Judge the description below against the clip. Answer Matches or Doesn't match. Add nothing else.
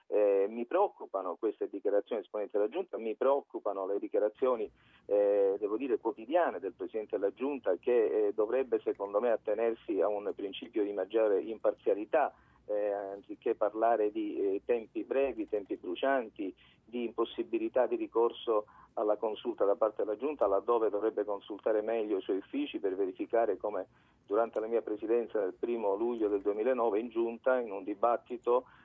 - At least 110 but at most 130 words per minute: Doesn't match